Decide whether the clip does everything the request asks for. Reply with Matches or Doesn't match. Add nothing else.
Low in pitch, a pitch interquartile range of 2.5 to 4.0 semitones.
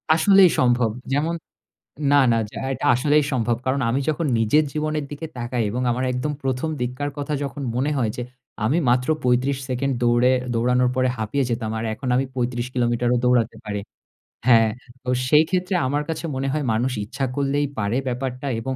Matches